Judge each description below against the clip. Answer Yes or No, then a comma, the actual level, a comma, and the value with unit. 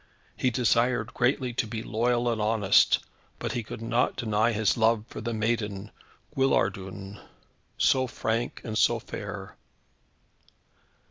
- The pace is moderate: No, slow, 130 wpm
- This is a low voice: Yes, low, 115 Hz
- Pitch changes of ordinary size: No, narrow, 2.0 semitones